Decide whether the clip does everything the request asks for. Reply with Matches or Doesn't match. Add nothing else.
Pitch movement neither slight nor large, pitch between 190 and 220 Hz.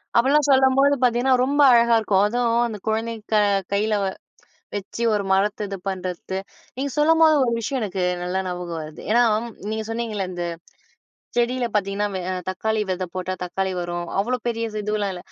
Matches